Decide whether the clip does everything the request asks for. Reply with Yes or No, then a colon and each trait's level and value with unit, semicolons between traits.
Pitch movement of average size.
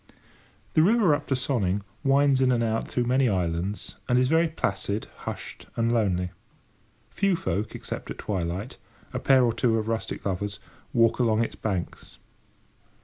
Yes: average, 4.7 semitones